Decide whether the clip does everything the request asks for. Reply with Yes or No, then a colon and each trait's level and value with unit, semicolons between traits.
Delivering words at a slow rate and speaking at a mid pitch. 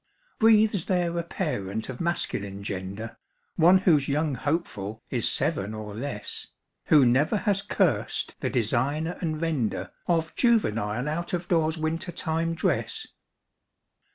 Yes: slow, 130 wpm; medium, 155 Hz